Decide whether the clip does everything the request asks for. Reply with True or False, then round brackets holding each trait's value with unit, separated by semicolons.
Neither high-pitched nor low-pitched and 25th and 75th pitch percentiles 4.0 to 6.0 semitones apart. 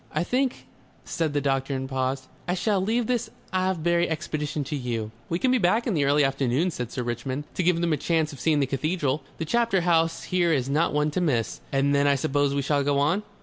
True (150 Hz; 4.3 semitones)